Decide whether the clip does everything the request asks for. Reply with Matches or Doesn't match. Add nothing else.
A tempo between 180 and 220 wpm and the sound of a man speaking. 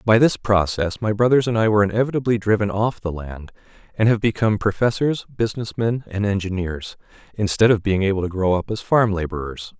Matches